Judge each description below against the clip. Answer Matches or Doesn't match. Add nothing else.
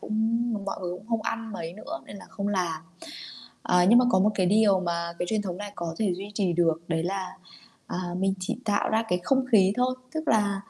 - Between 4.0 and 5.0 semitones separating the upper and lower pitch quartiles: Doesn't match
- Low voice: Doesn't match